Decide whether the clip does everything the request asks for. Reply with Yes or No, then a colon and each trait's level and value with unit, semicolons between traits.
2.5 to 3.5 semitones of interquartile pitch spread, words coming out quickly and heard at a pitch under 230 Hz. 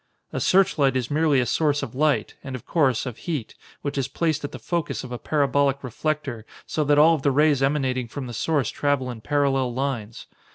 Yes: average, 2.8 semitones; fast, 210 wpm; medium, 140 Hz